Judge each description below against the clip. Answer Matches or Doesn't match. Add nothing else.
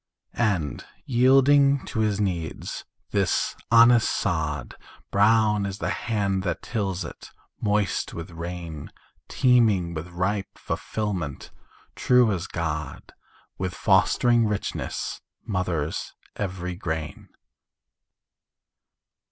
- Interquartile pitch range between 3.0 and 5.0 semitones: Matches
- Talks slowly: Matches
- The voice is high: Doesn't match